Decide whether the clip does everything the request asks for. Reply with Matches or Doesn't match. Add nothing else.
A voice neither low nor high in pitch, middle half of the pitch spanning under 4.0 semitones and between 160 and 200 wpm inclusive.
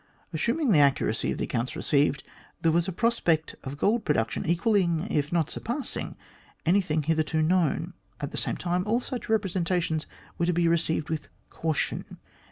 Matches